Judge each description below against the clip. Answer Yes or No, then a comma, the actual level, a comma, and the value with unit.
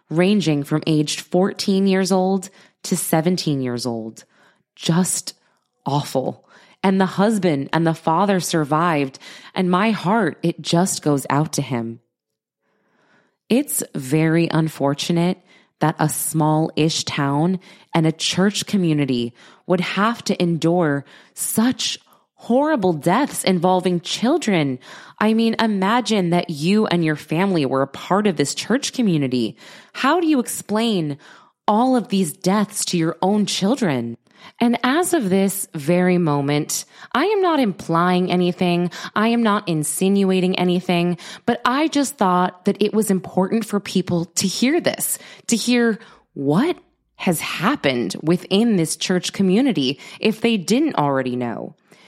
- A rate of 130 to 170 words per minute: Yes, slow, 135 wpm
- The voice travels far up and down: No, average, 4.5 semitones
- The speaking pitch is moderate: Yes, medium, 180 Hz